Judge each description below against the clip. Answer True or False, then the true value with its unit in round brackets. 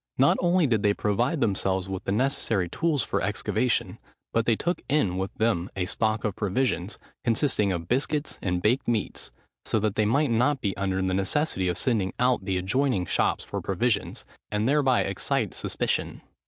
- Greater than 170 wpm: True (180 wpm)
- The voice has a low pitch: True (110 Hz)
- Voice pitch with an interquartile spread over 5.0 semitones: True (5.5 semitones)